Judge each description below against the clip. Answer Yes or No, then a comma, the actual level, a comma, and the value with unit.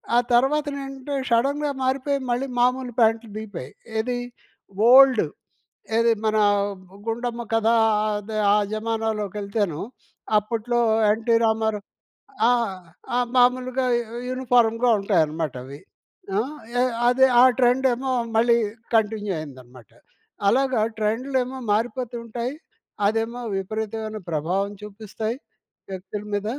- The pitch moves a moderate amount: Yes, average, 3.0 semitones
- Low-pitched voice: No, high, 225 Hz